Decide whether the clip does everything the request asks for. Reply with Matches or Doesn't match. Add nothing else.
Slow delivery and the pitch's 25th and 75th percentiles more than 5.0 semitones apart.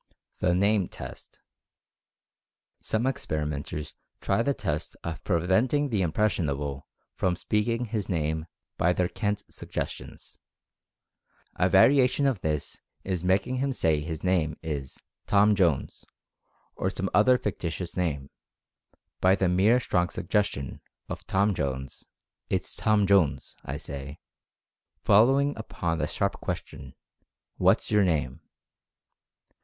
Matches